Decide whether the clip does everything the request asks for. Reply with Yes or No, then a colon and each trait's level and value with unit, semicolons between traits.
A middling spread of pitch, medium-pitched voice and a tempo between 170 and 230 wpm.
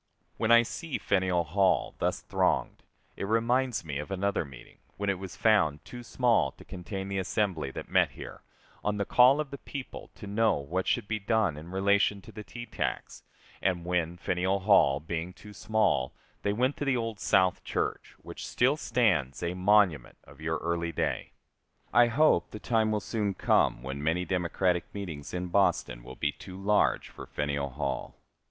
No: average, 4.5 semitones; very low, 95 Hz; average, 185 wpm